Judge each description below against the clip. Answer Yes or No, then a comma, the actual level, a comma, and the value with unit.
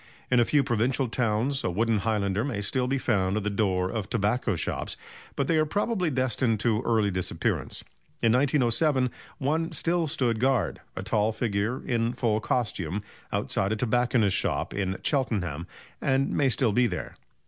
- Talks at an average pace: Yes, average, 170 wpm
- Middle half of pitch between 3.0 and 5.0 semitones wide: Yes, average, 4.2 semitones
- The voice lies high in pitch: No, low, 115 Hz